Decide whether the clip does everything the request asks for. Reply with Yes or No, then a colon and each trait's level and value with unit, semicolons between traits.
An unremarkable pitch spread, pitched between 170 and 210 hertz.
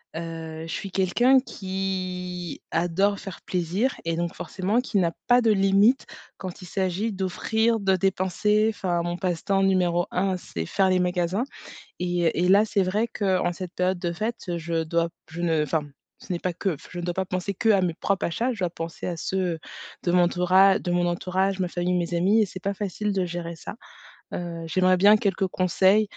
No: narrow, 2.2 semitones; medium, 185 Hz